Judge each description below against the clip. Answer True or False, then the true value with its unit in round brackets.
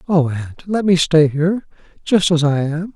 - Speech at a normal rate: True (180 wpm)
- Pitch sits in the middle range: True (165 Hz)